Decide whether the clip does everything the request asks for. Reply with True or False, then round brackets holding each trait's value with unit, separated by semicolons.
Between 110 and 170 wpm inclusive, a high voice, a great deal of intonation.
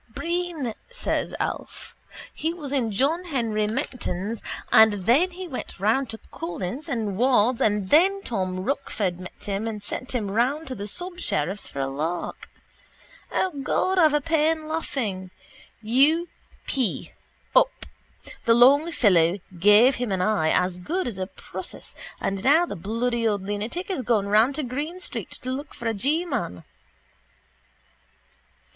True (150 wpm; 240 Hz; 6.9 semitones)